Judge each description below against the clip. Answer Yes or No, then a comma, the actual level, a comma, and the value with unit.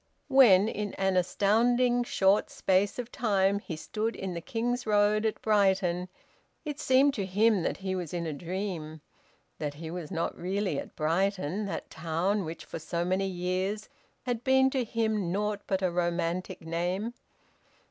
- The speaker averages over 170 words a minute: No, average, 165 wpm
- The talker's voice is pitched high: Yes, high, 195 Hz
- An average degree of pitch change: Yes, average, 3.6 semitones